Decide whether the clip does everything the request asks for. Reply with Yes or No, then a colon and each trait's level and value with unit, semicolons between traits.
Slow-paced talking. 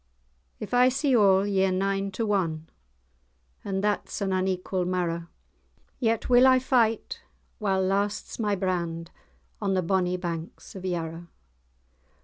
Yes: slow, 130 wpm